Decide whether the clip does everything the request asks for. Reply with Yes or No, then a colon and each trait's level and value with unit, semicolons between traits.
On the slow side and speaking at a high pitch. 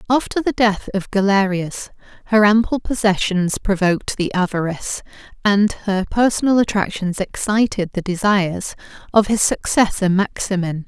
Yes: slow, 120 wpm; high, 200 Hz